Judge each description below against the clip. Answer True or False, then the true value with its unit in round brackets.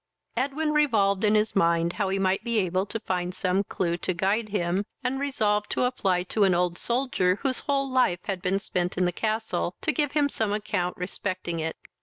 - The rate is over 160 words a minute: True (205 wpm)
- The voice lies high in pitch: True (200 Hz)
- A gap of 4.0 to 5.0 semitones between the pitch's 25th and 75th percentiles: True (4.5 semitones)